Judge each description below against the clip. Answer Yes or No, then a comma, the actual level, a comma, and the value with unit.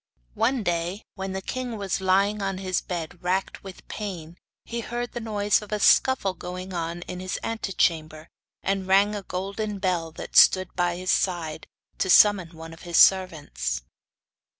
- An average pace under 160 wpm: No, average, 170 wpm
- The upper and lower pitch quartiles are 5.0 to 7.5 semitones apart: No, average, 2.8 semitones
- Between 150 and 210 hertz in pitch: Yes, medium, 185 Hz